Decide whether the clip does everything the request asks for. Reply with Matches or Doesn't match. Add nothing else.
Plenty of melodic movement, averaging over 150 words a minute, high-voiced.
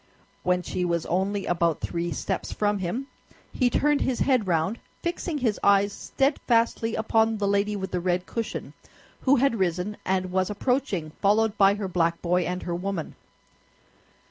Doesn't match